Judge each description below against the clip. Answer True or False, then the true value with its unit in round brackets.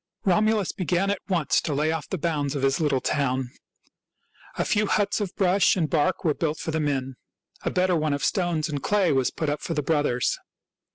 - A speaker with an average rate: False (210 wpm)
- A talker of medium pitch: True (155 Hz)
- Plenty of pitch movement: False (4.3 semitones)